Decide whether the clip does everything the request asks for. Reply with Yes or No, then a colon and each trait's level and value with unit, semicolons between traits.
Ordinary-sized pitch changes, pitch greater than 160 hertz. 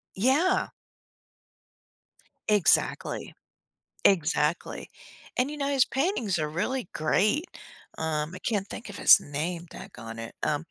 No: wide, 8.6 semitones; high, 190 Hz